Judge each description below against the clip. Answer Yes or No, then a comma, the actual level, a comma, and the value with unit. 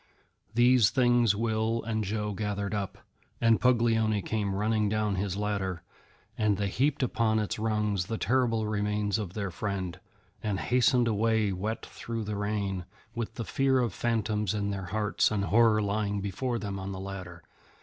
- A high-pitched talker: No, low, 105 Hz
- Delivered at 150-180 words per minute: Yes, average, 170 wpm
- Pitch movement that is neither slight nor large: No, narrow, 2.2 semitones